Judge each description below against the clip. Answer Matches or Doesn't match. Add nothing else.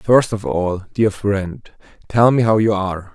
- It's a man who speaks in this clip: Matches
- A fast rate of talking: Doesn't match